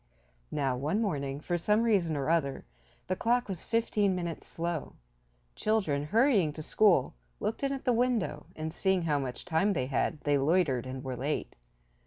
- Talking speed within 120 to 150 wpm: No, average, 175 wpm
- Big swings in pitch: Yes, wide, 6.6 semitones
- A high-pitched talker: No, medium, 165 Hz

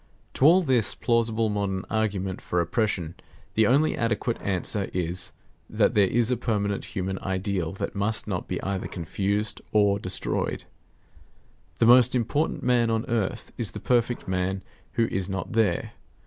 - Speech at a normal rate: Yes, average, 155 wpm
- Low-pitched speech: Yes, low, 105 Hz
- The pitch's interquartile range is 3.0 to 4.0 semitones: Yes, average, 3.5 semitones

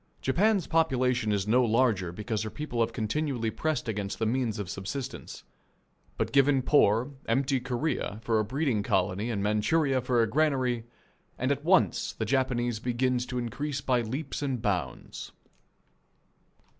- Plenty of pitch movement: No, average, 3.8 semitones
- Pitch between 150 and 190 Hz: No, low, 120 Hz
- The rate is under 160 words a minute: Yes, average, 150 wpm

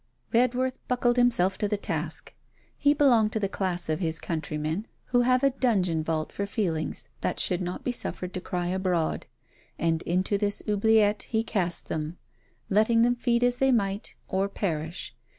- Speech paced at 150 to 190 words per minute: Yes, average, 170 wpm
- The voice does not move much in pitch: No, average, 5.3 semitones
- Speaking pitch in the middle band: No, high, 200 Hz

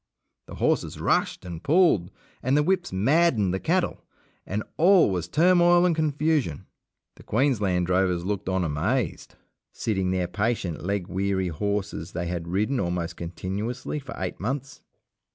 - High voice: No, low, 100 Hz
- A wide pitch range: Yes, wide, 8.0 semitones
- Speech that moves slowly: No, average, 145 wpm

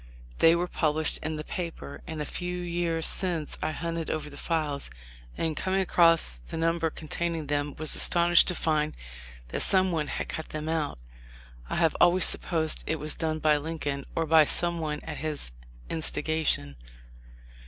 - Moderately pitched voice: Yes, medium, 160 Hz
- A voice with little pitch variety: Yes, narrow, 2.0 semitones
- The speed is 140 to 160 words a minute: No, average, 170 wpm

